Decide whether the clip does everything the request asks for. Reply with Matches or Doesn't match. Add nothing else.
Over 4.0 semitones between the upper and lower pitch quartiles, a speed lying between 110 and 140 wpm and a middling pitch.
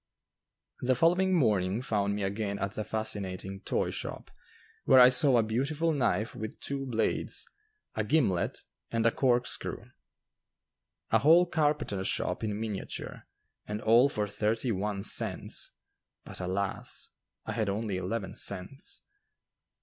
Doesn't match